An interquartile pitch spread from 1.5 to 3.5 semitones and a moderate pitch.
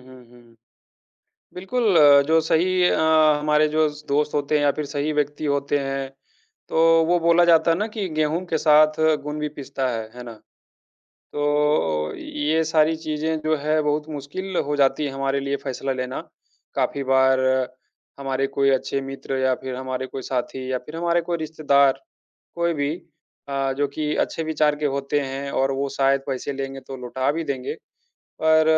Yes: narrow, 2.5 semitones; medium, 145 Hz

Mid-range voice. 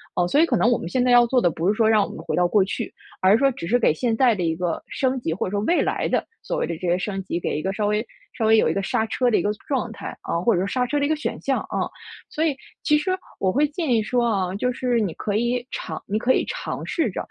No: high, 220 Hz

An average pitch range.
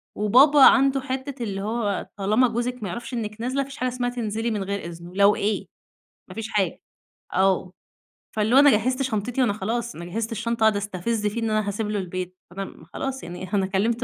Yes: average, 3.6 semitones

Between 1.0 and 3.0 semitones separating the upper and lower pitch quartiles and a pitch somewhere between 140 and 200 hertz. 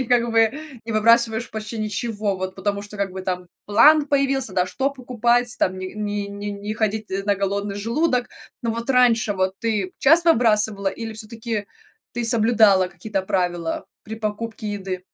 No: average, 2.7 semitones; high, 215 Hz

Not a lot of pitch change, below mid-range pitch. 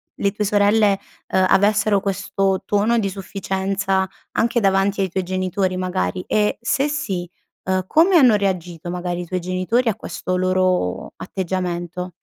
No: narrow, 2.0 semitones; high, 190 Hz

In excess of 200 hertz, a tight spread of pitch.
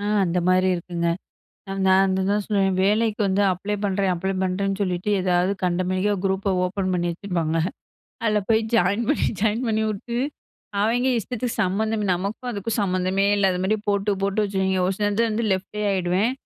No: high, 195 Hz; narrow, 2.3 semitones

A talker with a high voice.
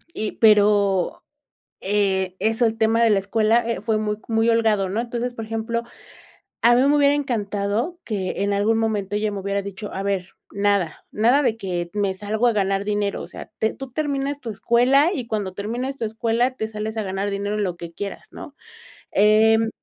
Yes: high, 215 Hz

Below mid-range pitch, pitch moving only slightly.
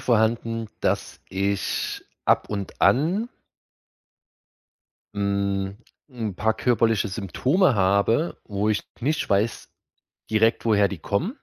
No: low, 110 Hz; average, 3.0 semitones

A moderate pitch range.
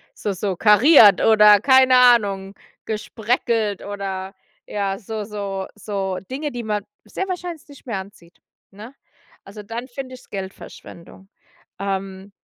Yes: average, 3.7 semitones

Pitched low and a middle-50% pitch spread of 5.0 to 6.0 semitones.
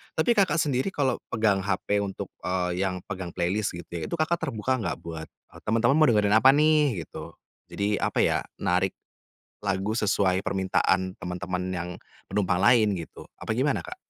Yes: low, 100 Hz; wide, 5.6 semitones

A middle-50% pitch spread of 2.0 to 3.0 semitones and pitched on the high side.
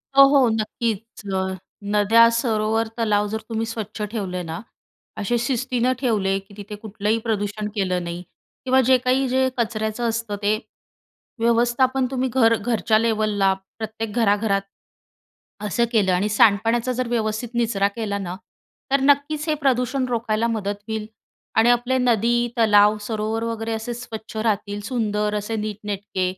Yes: narrow, 2.5 semitones; high, 220 Hz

